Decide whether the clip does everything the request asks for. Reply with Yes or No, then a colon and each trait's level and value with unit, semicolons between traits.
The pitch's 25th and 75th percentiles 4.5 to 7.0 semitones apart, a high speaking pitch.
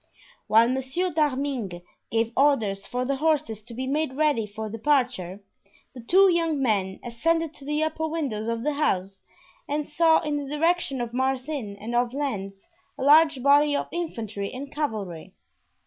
Yes: average, 5.1 semitones; very high, 265 Hz